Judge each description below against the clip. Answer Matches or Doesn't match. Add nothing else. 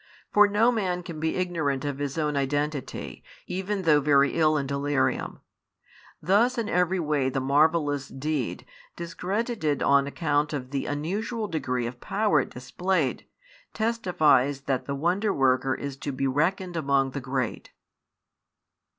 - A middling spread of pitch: Matches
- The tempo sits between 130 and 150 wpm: Matches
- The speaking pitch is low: Doesn't match